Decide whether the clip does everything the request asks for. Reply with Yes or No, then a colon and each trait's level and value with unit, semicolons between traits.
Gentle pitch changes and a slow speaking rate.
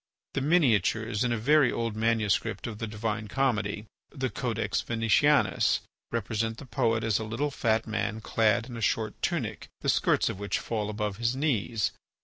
No: narrow, 2.1 semitones; average, 170 wpm